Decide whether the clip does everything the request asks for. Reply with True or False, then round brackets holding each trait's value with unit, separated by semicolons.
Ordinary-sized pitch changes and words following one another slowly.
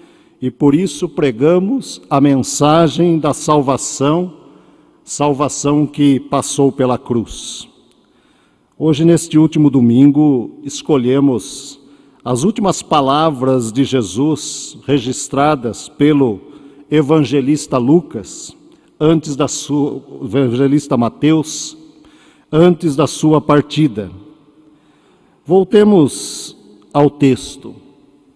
False (2.1 semitones; 85 wpm)